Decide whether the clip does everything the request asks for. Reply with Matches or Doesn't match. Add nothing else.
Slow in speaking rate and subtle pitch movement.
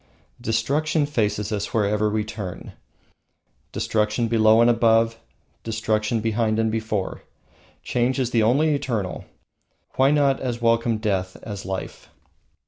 Matches